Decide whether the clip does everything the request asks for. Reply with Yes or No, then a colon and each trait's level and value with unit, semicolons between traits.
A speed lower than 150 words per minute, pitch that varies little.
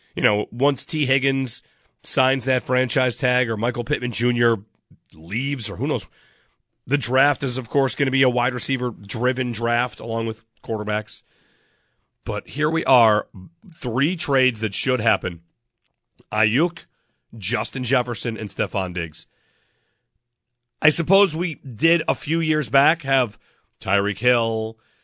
No: average, 140 wpm; average, 3.3 semitones